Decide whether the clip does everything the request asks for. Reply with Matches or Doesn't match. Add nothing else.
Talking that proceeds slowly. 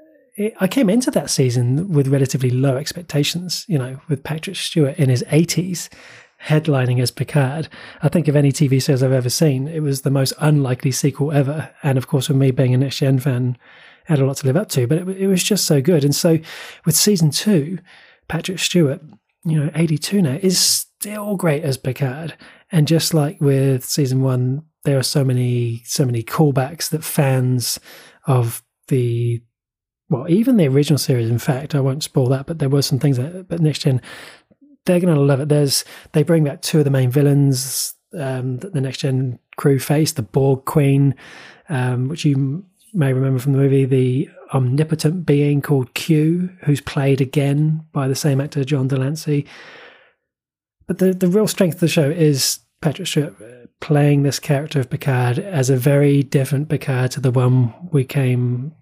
Doesn't match